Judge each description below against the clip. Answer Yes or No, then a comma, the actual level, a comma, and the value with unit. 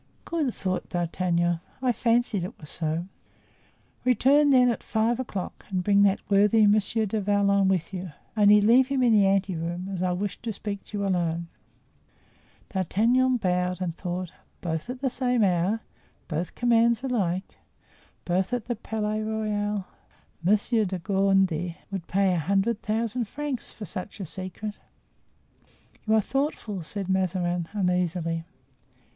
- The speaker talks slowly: No, average, 150 wpm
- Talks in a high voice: Yes, high, 200 Hz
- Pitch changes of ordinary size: Yes, average, 3.7 semitones